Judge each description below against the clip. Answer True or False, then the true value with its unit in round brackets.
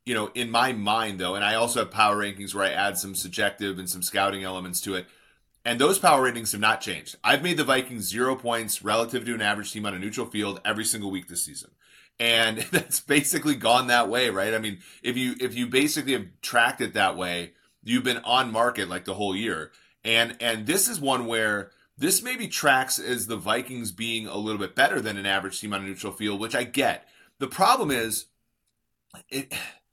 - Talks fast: True (220 wpm)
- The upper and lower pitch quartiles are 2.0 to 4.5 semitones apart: True (3.6 semitones)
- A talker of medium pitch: False (110 Hz)